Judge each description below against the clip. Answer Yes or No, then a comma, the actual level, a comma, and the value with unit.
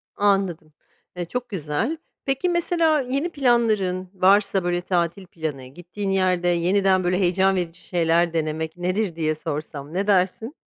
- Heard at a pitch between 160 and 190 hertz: Yes, medium, 185 Hz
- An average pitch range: Yes, average, 3.4 semitones